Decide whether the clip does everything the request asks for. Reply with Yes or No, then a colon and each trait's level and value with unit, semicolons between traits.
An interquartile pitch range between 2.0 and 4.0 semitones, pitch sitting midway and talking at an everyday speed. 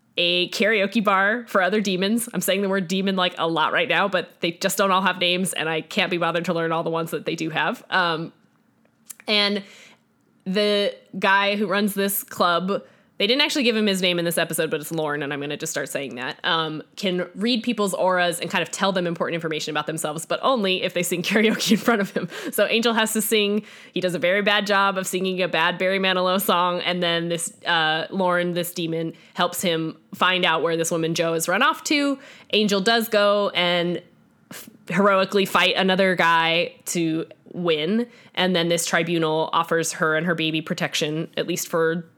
No: average, 3.4 semitones; medium, 180 Hz; fast, 215 wpm